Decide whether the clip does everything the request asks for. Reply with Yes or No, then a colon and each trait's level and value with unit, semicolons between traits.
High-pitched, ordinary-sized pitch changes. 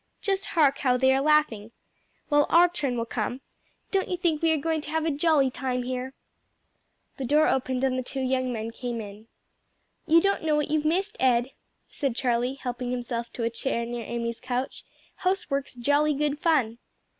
Yes: very high, 265 Hz; average, 3.9 semitones